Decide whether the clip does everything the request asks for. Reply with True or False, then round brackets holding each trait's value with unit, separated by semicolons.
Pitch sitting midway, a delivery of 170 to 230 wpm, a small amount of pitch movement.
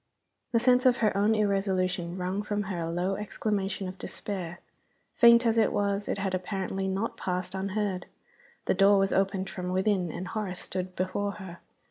False (195 Hz; 175 wpm; 2.0 semitones)